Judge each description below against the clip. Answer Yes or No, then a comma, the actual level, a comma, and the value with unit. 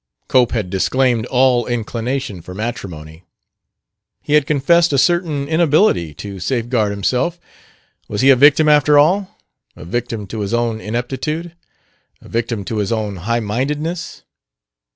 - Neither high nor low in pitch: No, low, 120 Hz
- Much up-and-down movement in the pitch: Yes, wide, 5.7 semitones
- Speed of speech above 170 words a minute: No, slow, 135 wpm